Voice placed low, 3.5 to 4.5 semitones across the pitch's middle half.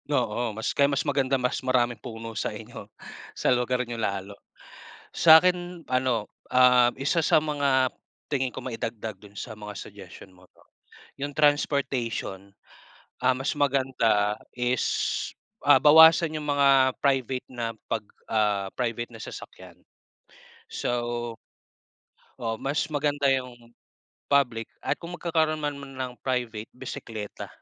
Yes: low, 130 Hz; average, 3.8 semitones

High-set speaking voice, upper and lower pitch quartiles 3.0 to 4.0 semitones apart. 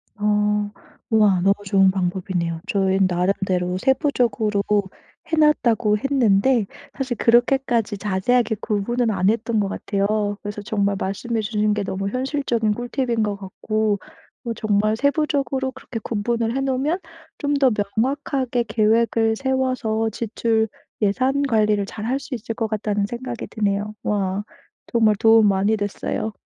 Yes: high, 220 Hz; average, 3.3 semitones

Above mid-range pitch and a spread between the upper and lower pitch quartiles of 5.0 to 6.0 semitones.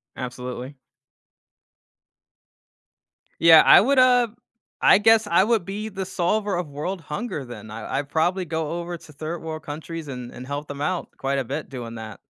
No: medium, 160 Hz; wide, 5.6 semitones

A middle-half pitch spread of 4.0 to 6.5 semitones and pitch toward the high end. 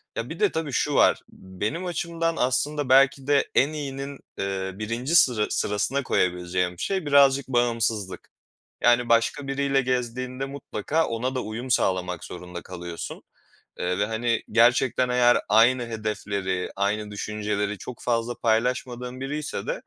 No: average, 4.7 semitones; low, 120 Hz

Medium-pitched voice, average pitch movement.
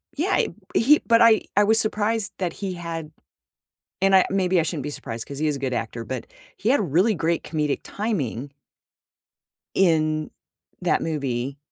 No: medium, 165 Hz; wide, 6.4 semitones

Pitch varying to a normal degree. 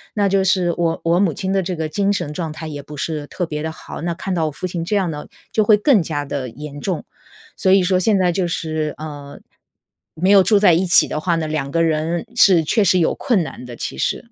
Yes: average, 3.6 semitones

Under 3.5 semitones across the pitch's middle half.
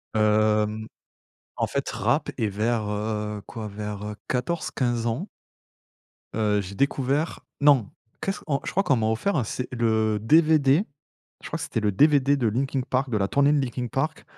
No: average, 4.6 semitones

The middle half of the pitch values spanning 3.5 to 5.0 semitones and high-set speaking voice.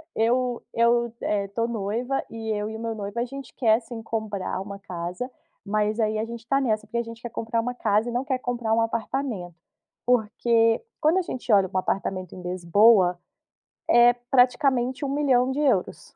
No: average, 3.0 semitones; high, 230 Hz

